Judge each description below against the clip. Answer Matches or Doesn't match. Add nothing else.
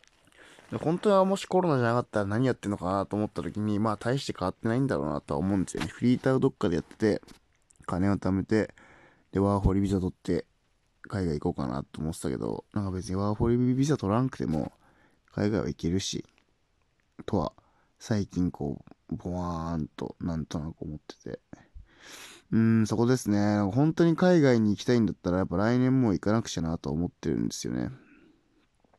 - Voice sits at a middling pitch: Doesn't match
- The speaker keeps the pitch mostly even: Doesn't match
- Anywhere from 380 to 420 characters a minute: Matches